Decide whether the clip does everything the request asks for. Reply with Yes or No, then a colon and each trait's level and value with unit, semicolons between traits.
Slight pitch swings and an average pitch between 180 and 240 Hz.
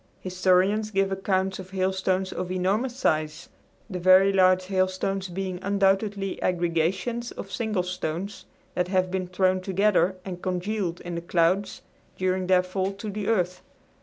Yes: narrow, 1.2 semitones; medium, 185 Hz